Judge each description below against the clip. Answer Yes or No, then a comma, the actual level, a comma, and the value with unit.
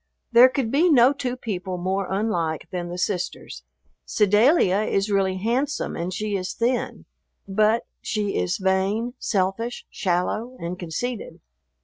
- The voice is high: Yes, high, 205 Hz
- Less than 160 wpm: Yes, slow, 135 wpm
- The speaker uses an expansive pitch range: No, average, 4.3 semitones